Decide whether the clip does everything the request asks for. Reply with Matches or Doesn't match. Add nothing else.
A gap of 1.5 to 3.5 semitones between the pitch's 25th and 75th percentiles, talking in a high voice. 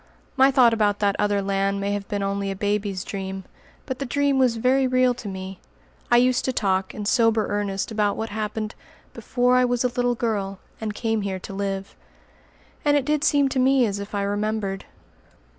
Doesn't match